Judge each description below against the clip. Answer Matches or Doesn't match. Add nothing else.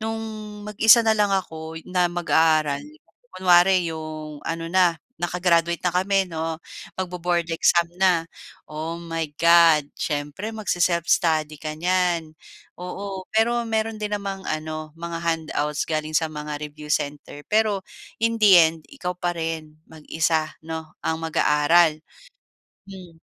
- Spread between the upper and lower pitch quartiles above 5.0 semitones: Doesn't match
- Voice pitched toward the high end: Doesn't match